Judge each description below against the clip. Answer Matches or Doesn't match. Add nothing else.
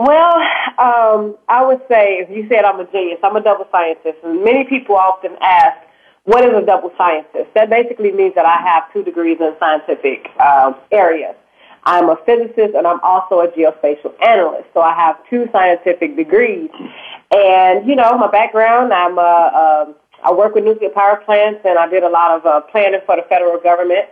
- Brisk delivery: Doesn't match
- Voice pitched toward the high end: Matches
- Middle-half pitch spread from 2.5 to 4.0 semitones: Doesn't match